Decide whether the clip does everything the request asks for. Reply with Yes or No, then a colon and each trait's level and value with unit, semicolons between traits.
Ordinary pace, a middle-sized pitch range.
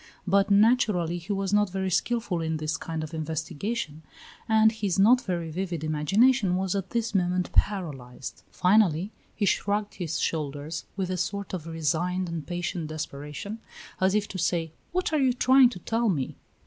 Yes: average, 170 wpm; average, 4.3 semitones